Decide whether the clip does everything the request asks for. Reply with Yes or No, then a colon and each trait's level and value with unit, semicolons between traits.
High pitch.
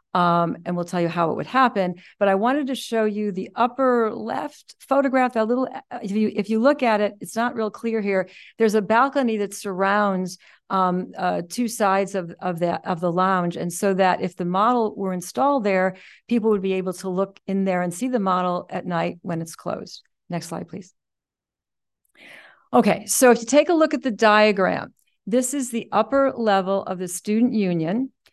Yes: high, 205 Hz